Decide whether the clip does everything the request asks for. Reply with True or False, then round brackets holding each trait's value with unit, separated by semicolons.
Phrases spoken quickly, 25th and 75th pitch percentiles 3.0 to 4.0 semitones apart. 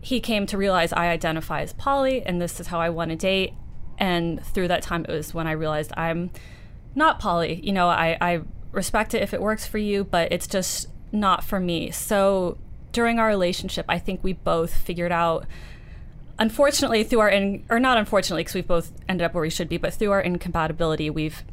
True (210 wpm; 3.4 semitones)